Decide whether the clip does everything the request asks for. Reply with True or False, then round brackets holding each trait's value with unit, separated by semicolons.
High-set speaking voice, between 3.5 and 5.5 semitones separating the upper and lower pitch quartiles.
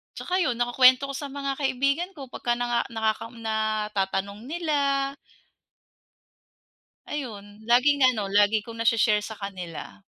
True (235 Hz; 4.6 semitones)